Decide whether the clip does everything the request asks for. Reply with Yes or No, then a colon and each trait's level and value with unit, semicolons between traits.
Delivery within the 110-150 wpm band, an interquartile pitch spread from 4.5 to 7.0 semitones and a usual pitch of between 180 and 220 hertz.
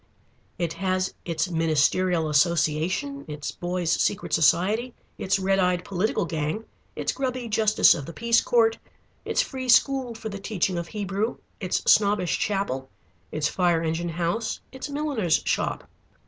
Yes: average, 145 wpm; average, 5.0 semitones; medium, 185 Hz